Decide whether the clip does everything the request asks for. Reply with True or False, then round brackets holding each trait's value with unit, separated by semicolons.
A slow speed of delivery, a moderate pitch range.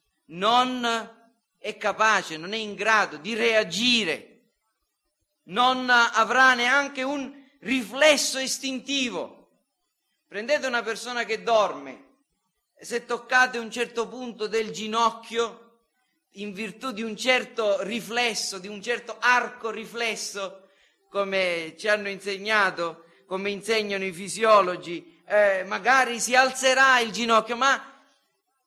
True (110 wpm; 3.4 semitones)